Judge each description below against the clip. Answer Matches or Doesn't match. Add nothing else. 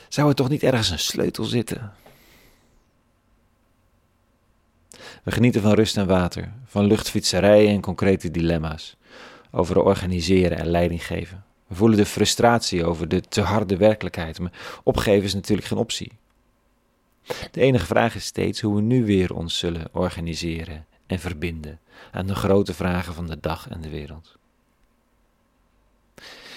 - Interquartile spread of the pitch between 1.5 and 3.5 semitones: Doesn't match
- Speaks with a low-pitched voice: Matches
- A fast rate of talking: Doesn't match